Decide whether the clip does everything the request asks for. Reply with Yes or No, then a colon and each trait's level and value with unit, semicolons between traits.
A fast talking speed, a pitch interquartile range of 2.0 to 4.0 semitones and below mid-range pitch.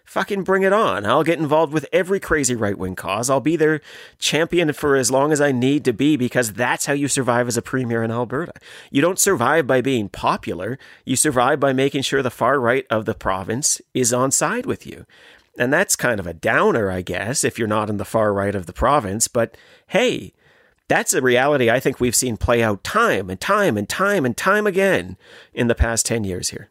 No: fast, 225 wpm; average, 4.9 semitones; low, 130 Hz